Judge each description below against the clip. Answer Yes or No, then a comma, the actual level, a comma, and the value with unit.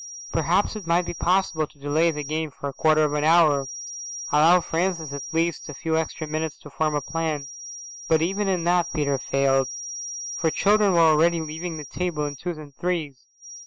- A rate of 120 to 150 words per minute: No, average, 195 wpm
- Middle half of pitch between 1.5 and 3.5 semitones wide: Yes, narrow, 2.5 semitones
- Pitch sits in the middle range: Yes, medium, 160 Hz